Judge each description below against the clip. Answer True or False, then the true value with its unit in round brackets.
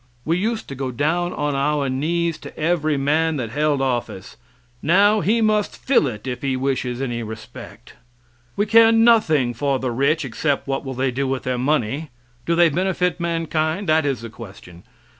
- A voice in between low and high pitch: True (145 Hz)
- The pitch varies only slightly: False (4.7 semitones)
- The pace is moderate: True (180 wpm)